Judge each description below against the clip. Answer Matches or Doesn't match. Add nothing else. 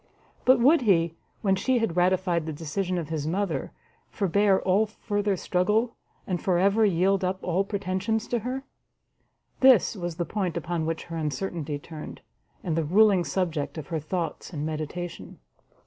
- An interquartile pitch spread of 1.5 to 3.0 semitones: Doesn't match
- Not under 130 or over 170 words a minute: Matches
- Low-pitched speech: Doesn't match